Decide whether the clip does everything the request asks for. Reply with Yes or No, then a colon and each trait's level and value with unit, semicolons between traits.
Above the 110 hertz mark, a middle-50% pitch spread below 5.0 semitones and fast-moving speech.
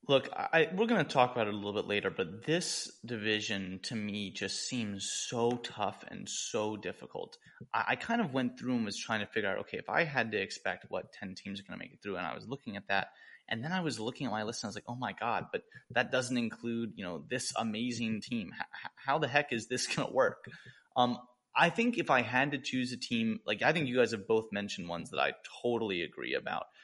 Yes: low, 120 Hz; average, 3.7 semitones; fast, 255 wpm